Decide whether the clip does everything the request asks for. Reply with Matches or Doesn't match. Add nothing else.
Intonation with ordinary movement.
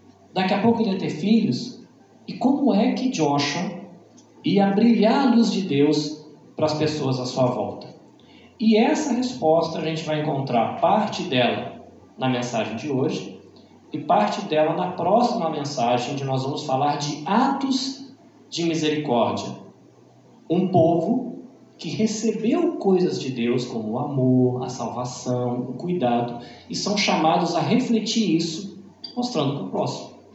Doesn't match